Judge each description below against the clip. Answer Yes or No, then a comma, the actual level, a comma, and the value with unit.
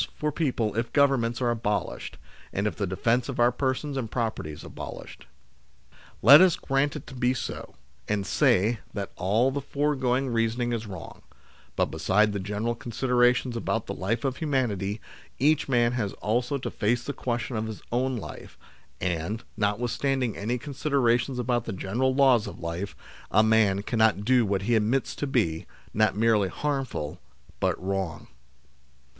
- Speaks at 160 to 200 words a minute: Yes, average, 165 wpm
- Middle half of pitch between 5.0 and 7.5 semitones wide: No, average, 3.9 semitones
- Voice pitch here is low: Yes, low, 120 Hz